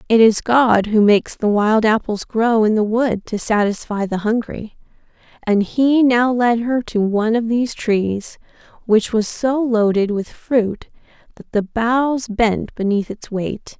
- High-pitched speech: Yes, high, 225 Hz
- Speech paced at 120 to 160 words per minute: No, average, 170 wpm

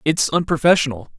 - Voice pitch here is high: No, medium, 150 Hz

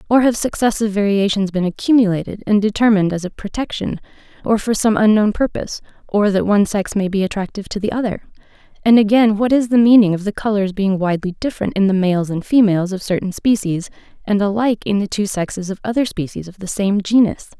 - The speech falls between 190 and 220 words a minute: Yes, average, 200 wpm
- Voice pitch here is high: Yes, high, 205 Hz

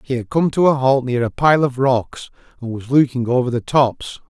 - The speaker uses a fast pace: Yes, fast, 235 wpm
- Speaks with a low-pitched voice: Yes, low, 130 Hz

